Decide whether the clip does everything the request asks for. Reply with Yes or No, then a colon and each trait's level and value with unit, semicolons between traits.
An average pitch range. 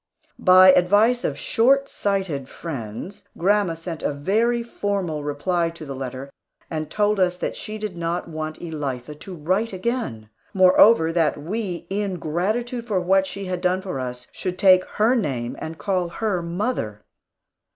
Yes: average, 4.7 semitones